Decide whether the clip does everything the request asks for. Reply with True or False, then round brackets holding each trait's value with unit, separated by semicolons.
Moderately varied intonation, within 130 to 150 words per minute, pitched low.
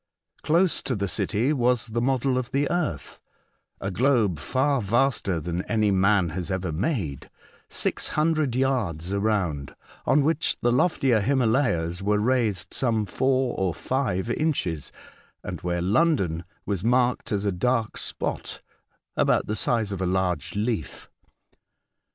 False (5.9 semitones; 140 wpm; 110 Hz)